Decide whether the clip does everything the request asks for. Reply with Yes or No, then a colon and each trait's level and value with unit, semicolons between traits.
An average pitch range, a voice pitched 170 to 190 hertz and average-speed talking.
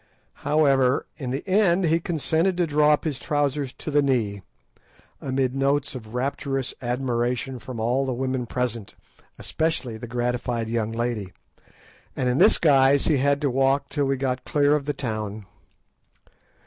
No: average, 3.0 semitones; low, 135 Hz; average, 160 wpm